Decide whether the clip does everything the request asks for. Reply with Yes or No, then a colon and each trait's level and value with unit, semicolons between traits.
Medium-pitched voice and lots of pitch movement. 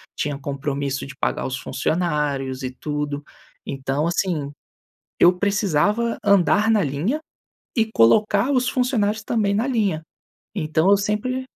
Yes: medium, 180 Hz; wide, 6.9 semitones